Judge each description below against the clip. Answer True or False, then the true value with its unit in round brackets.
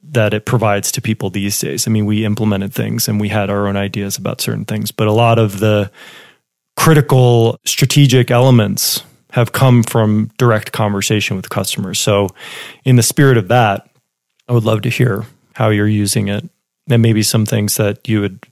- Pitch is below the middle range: True (110 Hz)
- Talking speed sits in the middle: True (190 wpm)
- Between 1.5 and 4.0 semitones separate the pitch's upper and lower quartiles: True (2.8 semitones)